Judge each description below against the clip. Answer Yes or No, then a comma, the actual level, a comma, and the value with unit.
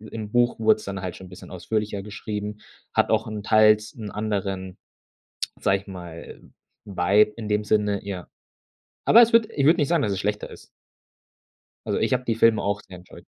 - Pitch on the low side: Yes, low, 105 Hz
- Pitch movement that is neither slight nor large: No, narrow, 2.0 semitones